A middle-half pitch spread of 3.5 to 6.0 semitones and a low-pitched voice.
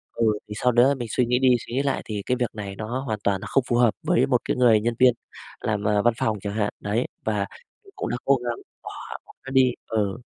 No: average, 3.0 semitones; low, 120 Hz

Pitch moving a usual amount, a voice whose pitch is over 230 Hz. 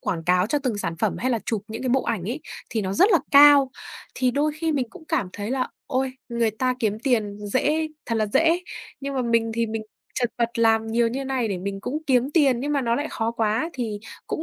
Yes: average, 3.8 semitones; high, 240 Hz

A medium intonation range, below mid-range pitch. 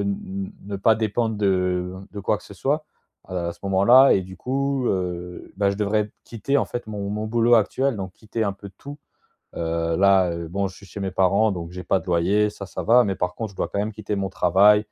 Yes: average, 3.1 semitones; low, 100 Hz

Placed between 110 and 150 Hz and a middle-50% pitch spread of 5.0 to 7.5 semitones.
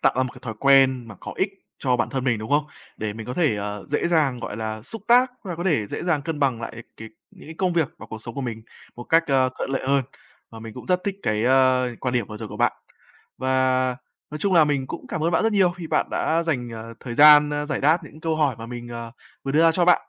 Yes: low, 135 Hz; average, 5.3 semitones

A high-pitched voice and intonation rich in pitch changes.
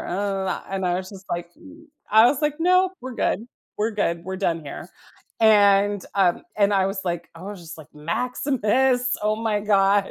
No: high, 205 Hz; average, 3.6 semitones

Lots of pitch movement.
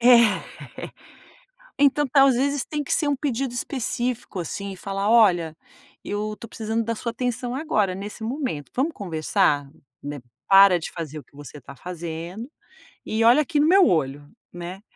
Yes: wide, 6.7 semitones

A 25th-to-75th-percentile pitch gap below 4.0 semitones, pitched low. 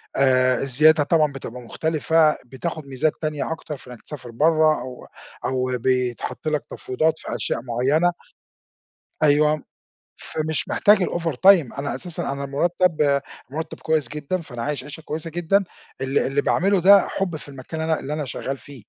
No: average, 3.3 semitones; medium, 150 Hz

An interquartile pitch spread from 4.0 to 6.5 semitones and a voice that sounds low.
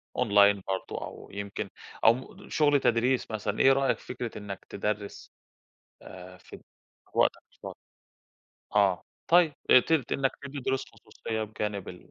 Yes: average, 4.7 semitones; low, 110 Hz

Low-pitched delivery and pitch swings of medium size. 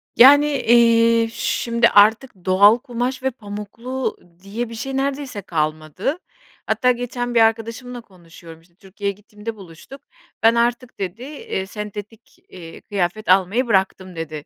No: high, 225 Hz; average, 4.3 semitones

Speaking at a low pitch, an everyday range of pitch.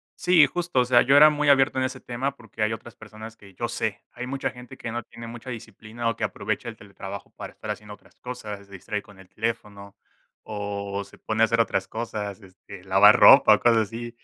Yes: low, 110 Hz; average, 3.1 semitones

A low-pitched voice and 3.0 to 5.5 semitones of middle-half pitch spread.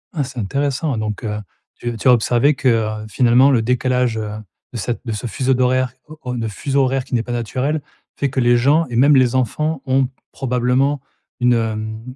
No: low, 125 Hz; narrow, 2.6 semitones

